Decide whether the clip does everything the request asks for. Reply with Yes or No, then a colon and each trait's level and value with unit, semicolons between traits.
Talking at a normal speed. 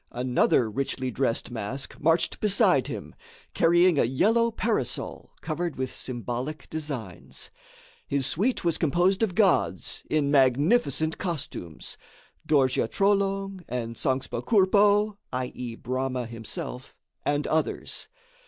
No: slow, 110 wpm